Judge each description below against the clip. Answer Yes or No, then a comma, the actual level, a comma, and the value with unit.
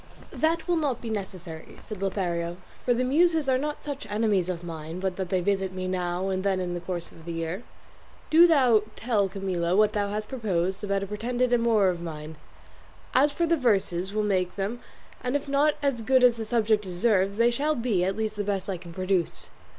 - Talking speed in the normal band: No, fast, 210 wpm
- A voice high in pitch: Yes, high, 200 Hz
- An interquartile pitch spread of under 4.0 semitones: No, average, 4.9 semitones